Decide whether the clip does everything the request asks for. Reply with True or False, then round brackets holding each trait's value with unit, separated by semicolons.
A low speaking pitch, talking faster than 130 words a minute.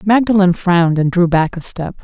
False (180 Hz; 205 wpm)